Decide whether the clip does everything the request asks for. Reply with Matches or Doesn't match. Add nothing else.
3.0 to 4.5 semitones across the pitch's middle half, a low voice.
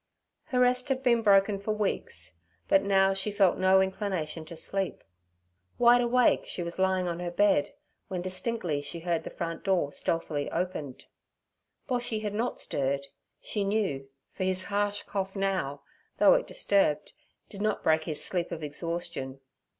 Doesn't match